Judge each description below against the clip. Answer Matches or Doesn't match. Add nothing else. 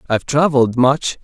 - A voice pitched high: Doesn't match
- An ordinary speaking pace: Matches